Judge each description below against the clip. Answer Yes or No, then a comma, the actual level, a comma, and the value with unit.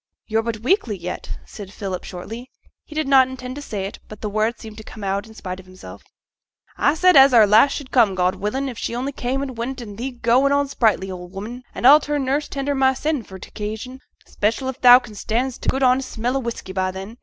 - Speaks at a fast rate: Yes, fast, 240 wpm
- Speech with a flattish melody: No, average, 4.3 semitones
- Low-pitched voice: No, high, 235 Hz